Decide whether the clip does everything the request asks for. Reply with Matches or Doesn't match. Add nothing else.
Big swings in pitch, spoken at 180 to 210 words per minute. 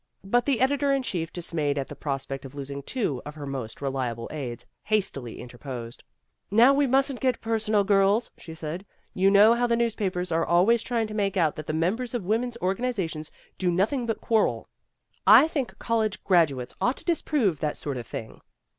Matches